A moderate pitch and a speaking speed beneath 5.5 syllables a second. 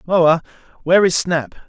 Yes: medium, 170 Hz; 5.0 syllables/s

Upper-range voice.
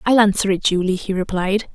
Yes: high, 195 Hz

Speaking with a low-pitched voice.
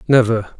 Yes: low, 115 Hz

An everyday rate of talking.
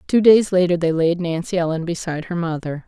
No: fast, 210 wpm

